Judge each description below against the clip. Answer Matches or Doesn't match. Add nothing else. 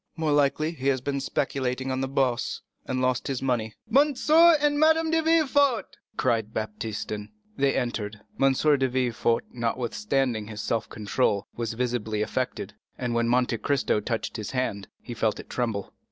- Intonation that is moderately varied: Matches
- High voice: Doesn't match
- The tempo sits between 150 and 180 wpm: Matches